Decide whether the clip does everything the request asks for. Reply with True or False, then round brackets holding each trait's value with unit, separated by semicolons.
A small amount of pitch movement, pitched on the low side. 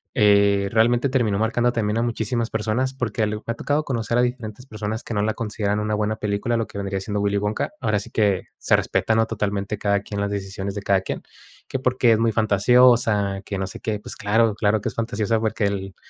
True (2.3 semitones; 110 Hz)